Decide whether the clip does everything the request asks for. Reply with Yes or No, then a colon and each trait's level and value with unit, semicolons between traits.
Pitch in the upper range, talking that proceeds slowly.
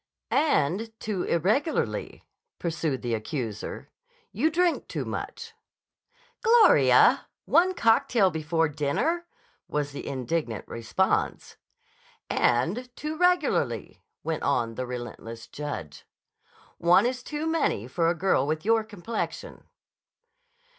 No: medium, 170 Hz; slow, 110 wpm